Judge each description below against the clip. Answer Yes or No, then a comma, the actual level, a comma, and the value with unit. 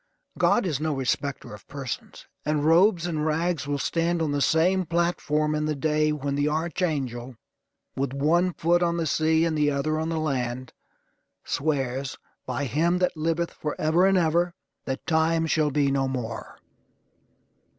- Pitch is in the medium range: Yes, medium, 155 Hz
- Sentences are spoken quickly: No, average, 160 wpm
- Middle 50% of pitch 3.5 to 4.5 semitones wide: No, average, 3.0 semitones